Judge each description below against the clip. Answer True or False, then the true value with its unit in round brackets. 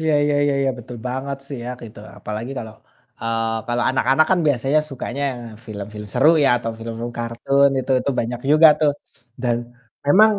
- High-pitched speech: False (125 Hz)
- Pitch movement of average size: True (3.5 semitones)